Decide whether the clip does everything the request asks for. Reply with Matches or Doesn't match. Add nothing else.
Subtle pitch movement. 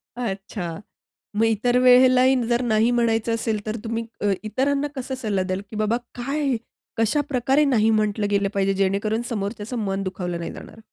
Doesn't match